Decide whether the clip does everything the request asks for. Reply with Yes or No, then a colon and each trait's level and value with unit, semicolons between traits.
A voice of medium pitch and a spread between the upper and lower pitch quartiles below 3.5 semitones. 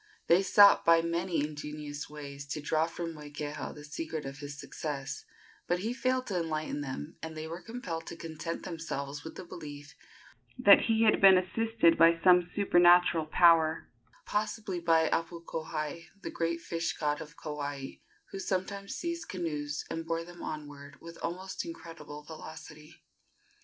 Yes: medium, 165 Hz; average, 3.0 semitones